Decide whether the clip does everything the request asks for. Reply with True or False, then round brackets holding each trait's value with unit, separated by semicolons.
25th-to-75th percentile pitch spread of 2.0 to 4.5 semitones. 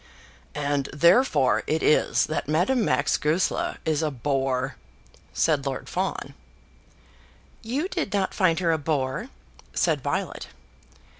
False (4.9 semitones)